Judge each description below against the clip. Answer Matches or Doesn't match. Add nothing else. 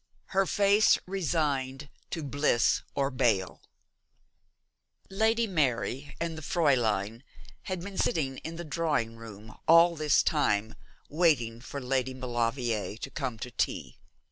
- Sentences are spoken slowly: Matches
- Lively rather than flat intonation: Matches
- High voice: Doesn't match